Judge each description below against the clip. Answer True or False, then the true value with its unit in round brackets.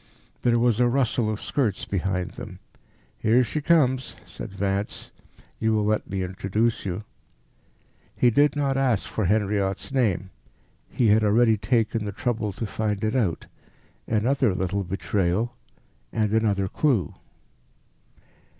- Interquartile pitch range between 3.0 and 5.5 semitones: True (3.6 semitones)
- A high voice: False (110 Hz)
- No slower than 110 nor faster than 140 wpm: True (135 wpm)